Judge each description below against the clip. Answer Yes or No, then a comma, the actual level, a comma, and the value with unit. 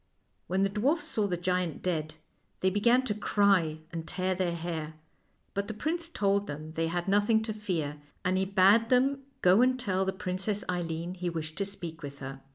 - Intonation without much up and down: No, average, 3.8 semitones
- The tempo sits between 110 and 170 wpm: No, average, 200 wpm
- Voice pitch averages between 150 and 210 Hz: Yes, medium, 185 Hz